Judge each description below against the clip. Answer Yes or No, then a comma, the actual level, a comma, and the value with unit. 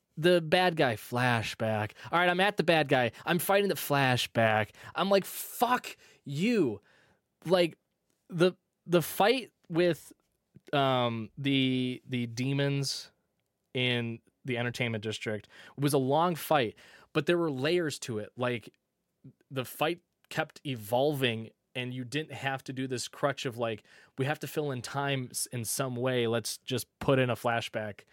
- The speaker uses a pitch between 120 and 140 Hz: Yes, low, 135 Hz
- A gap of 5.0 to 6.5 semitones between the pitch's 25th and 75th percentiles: Yes, average, 5.3 semitones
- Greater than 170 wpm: No, average, 155 wpm